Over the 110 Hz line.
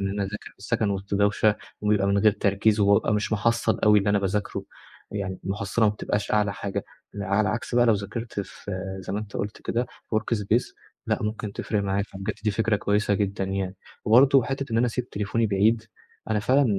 No: low, 105 Hz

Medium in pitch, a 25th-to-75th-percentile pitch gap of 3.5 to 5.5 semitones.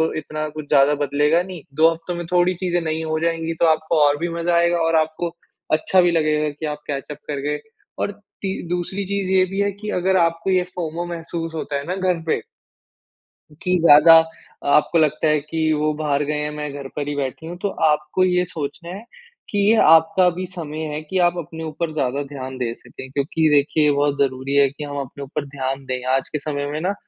No: medium, 155 Hz; average, 3.0 semitones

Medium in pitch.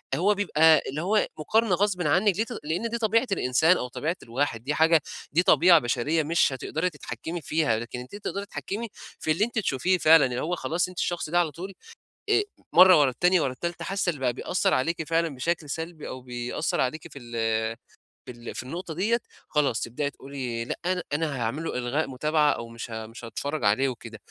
Yes: medium, 155 Hz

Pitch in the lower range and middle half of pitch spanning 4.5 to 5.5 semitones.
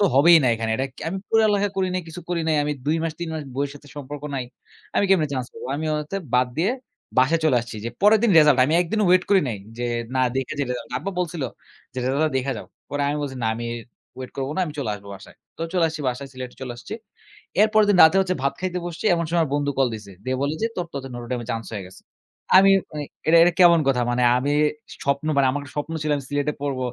No: medium, 145 Hz; average, 4.9 semitones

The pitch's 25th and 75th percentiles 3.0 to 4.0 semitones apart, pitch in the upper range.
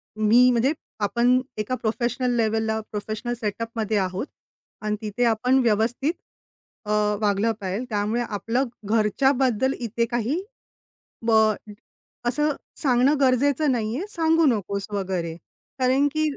Yes: average, 3.3 semitones; high, 230 Hz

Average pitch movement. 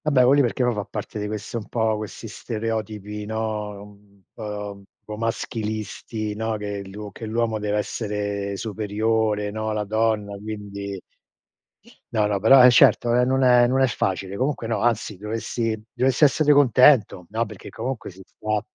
No: narrow, 2.1 semitones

